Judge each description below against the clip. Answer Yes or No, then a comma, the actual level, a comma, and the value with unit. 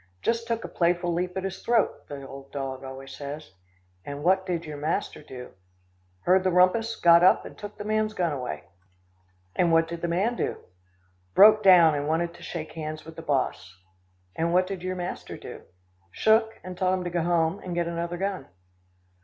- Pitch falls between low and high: Yes, medium, 175 Hz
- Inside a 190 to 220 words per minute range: Yes, average, 195 wpm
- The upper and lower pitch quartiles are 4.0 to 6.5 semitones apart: No, average, 3.3 semitones